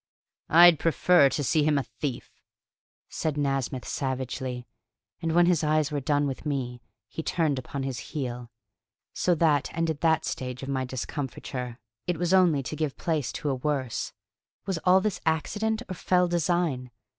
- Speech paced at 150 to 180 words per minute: Yes, average, 165 wpm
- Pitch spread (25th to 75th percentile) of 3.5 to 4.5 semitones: Yes, average, 4.0 semitones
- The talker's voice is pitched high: No, medium, 150 Hz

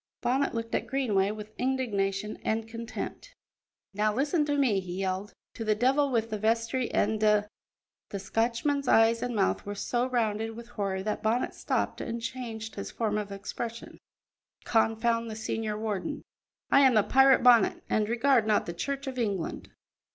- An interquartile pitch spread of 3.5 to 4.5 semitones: No, average, 2.8 semitones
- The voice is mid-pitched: No, high, 225 Hz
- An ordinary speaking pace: Yes, average, 175 wpm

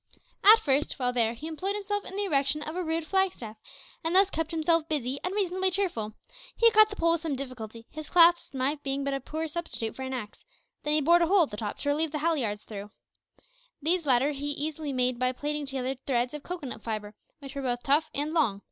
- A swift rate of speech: Yes, fast, 230 wpm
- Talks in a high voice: Yes, very high, 295 Hz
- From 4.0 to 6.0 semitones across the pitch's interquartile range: Yes, average, 4.7 semitones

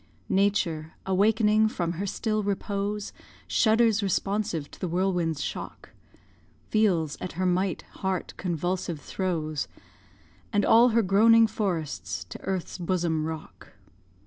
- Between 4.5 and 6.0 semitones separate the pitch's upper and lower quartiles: No, average, 4.1 semitones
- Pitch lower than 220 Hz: Yes, high, 190 Hz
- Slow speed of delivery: Yes, slow, 120 wpm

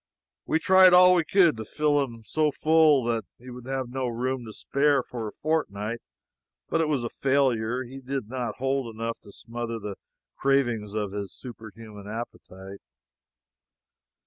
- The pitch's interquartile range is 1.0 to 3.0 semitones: No, average, 3.9 semitones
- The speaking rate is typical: Yes, average, 165 wpm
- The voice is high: No, low, 125 Hz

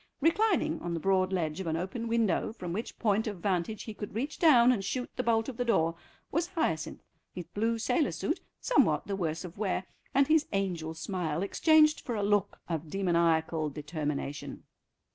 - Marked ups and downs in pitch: Yes, wide, 6.0 semitones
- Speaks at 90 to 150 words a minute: No, average, 185 wpm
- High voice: Yes, high, 195 Hz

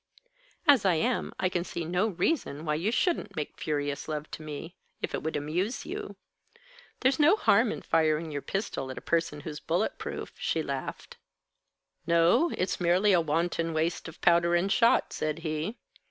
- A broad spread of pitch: No, average, 4.0 semitones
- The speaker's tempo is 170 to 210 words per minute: Yes, average, 180 wpm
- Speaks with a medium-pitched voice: Yes, medium, 170 Hz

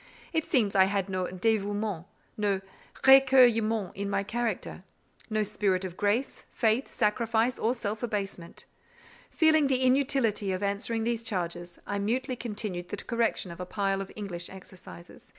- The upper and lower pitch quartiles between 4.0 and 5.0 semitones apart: No, average, 3.3 semitones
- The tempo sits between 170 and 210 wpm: No, average, 150 wpm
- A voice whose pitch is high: Yes, high, 210 Hz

